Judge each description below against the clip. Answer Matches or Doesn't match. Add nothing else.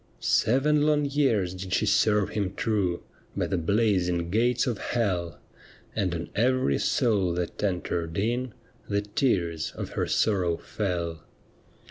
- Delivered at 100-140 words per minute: Matches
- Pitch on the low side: Matches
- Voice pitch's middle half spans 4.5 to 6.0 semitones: Matches